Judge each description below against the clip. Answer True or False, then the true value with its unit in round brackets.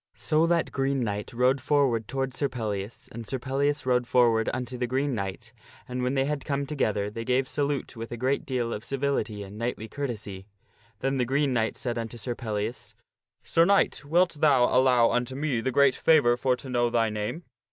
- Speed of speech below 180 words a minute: False (205 wpm)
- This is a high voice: False (125 Hz)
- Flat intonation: False (3.2 semitones)